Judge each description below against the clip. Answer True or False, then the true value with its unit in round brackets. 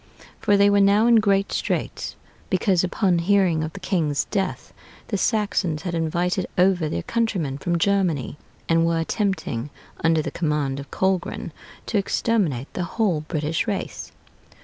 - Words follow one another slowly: False (150 wpm)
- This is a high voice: False (180 Hz)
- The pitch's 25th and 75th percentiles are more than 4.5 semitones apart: False (4.0 semitones)